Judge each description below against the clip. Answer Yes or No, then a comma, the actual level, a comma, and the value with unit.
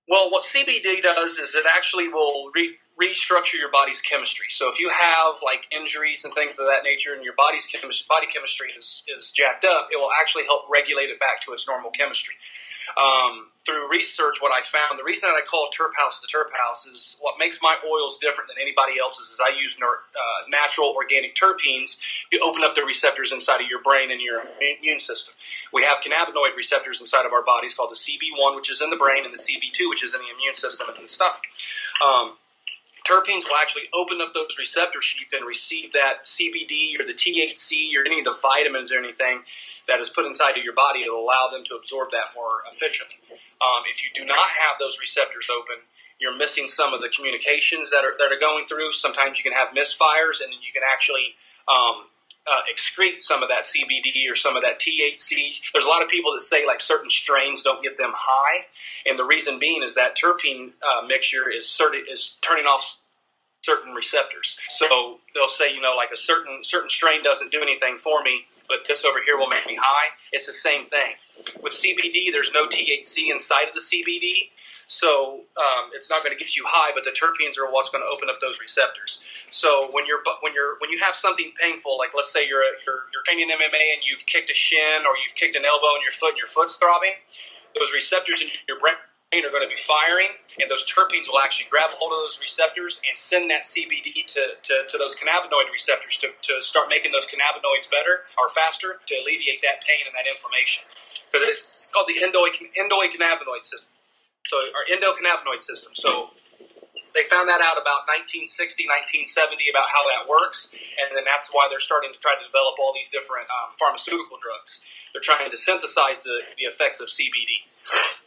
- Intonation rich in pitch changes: Yes, wide, 8.2 semitones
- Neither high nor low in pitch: Yes, medium, 160 Hz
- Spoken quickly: Yes, fast, 210 wpm